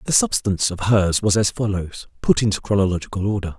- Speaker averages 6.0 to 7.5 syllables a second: Yes, 6.1 syllables/s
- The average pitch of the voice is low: Yes, low, 100 Hz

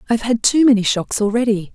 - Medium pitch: No, high, 225 Hz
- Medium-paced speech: No, fast, 240 wpm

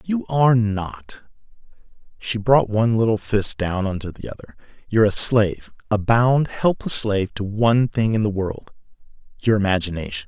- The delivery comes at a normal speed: Yes, average, 160 wpm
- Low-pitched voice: Yes, low, 105 Hz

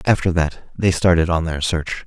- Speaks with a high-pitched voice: No, very low, 85 Hz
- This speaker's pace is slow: No, fast, 205 wpm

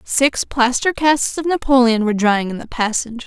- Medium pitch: No, very high, 250 Hz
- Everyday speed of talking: Yes, average, 185 wpm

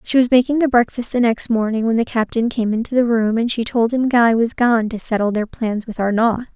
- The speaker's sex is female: Yes, female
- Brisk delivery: Yes, fast, 255 wpm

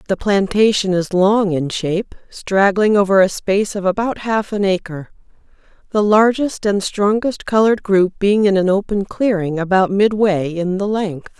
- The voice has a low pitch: No, high, 200 Hz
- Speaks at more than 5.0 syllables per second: No, 4.6 syllables/s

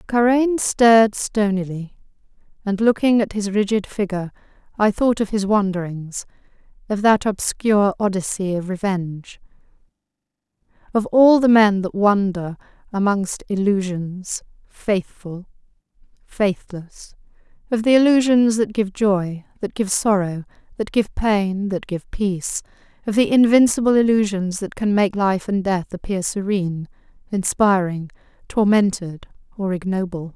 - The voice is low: No, high, 200 Hz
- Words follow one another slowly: Yes, slow, 120 wpm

